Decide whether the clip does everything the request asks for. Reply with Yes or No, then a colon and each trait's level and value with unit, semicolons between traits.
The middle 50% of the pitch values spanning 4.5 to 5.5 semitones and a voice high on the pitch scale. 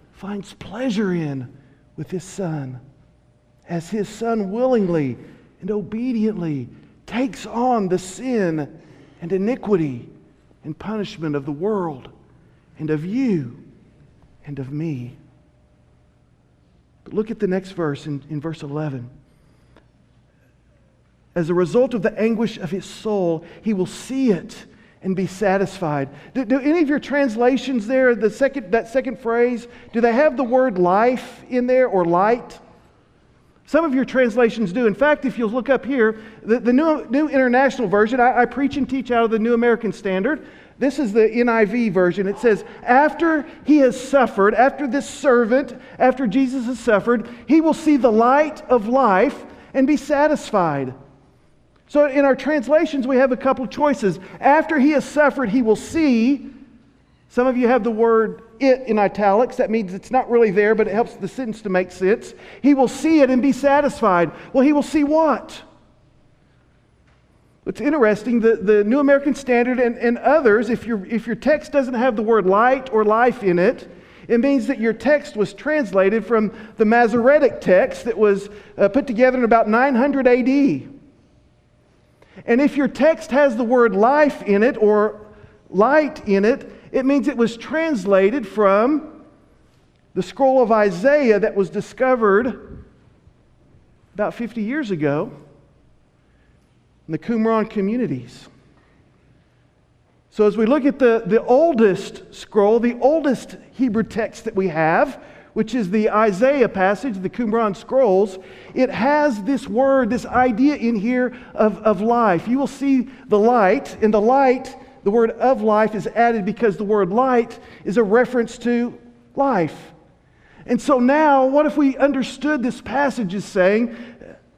Yes: average, 4.9 semitones; high, 230 Hz